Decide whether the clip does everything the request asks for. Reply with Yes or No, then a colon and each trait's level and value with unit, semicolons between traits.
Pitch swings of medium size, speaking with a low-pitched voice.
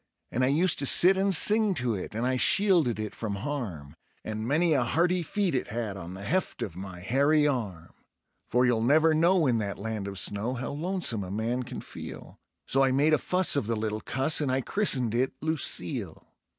No: wide, 6.6 semitones; low, 130 Hz